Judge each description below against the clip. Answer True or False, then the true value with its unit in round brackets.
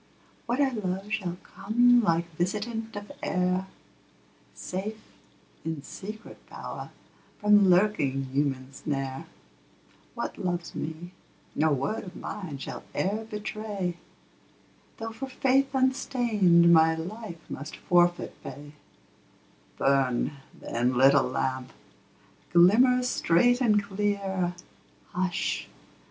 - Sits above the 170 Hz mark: True (185 Hz)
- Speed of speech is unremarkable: False (105 wpm)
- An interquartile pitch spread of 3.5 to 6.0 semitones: True (5.0 semitones)